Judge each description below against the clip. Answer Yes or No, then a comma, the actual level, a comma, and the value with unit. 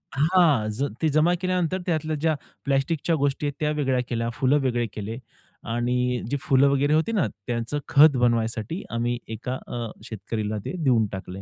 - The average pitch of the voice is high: No, low, 135 Hz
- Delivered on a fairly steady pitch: No, average, 4.7 semitones